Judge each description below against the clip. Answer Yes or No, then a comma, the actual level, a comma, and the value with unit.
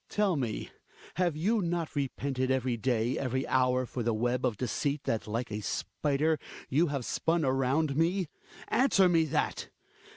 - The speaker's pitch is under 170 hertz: Yes, low, 135 Hz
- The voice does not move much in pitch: No, average, 4.4 semitones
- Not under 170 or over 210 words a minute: No, average, 160 wpm